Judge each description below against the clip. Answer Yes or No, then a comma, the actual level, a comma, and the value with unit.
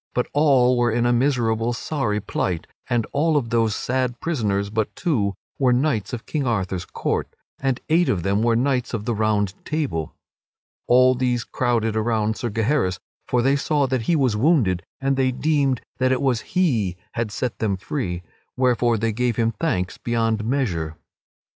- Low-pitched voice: Yes, low, 120 Hz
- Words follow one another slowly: No, average, 175 wpm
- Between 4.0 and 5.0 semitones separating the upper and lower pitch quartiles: No, average, 3.6 semitones